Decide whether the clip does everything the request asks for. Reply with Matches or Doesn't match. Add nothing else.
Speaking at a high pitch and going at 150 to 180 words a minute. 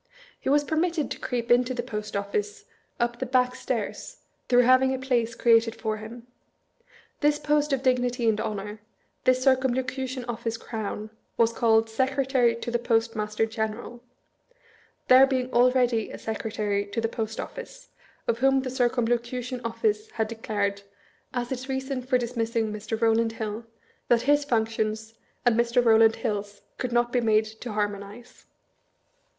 Matches